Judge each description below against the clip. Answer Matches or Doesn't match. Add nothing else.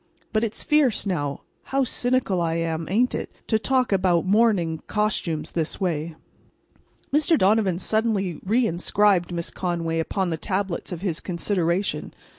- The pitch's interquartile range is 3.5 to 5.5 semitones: Matches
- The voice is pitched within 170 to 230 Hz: Matches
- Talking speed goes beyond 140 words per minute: Doesn't match